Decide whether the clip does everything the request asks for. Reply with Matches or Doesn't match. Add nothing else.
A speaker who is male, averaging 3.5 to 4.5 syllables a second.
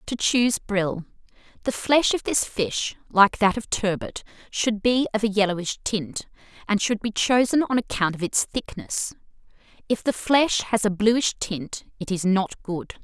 Doesn't match